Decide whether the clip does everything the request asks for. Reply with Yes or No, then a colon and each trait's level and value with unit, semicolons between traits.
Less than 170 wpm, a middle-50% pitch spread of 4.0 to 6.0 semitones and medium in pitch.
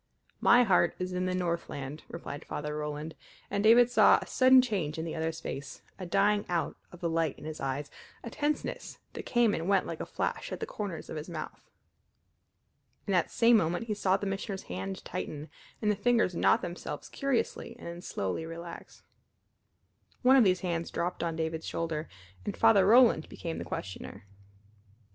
No: average, 185 wpm; average, 4.6 semitones; medium, 175 Hz